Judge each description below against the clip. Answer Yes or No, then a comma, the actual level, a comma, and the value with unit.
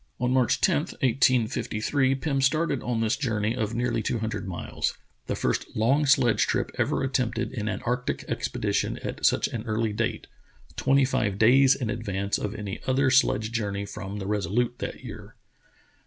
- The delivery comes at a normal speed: Yes, average, 175 wpm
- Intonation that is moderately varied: Yes, average, 3.6 semitones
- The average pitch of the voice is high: No, low, 120 Hz